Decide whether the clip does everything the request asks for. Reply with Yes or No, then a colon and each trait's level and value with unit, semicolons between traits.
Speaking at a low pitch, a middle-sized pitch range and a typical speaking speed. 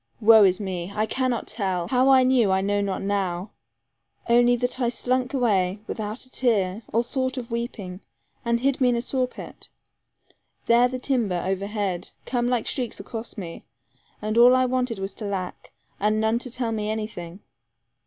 No: high, 225 Hz; average, 4.0 semitones; average, 185 wpm